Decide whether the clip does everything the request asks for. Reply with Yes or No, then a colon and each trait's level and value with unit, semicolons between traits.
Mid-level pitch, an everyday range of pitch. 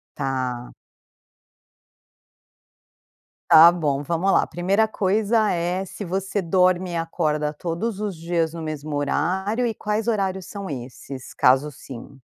Yes: medium, 175 Hz; average, 4.6 semitones